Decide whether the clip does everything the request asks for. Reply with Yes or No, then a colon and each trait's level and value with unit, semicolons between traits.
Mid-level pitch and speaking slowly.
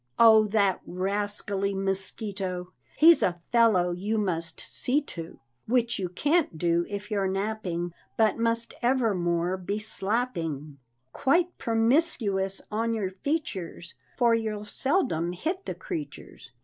No: high, 205 Hz; slow, 125 wpm